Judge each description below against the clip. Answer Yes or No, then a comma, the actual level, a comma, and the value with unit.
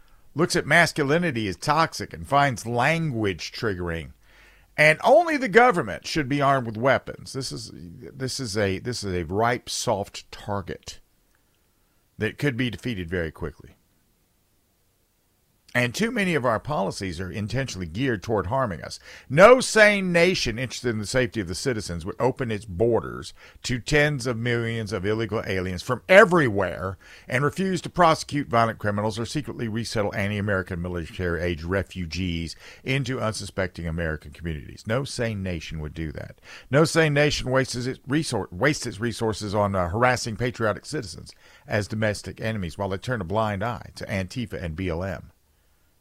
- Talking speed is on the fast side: No, average, 150 wpm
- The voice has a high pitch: No, low, 110 Hz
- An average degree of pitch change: No, wide, 5.9 semitones